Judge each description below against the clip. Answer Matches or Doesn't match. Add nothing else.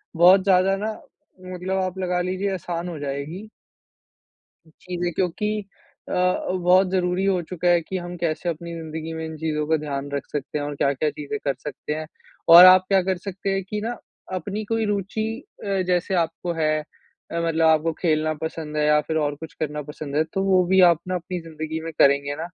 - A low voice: Doesn't match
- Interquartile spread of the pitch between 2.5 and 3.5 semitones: Matches